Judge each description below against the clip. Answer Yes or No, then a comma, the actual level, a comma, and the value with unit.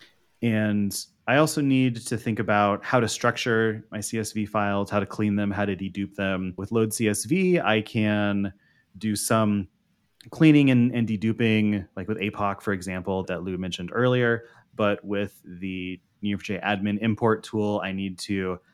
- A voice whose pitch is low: Yes, low, 105 Hz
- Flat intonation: Yes, narrow, 2.2 semitones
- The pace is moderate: Yes, average, 165 wpm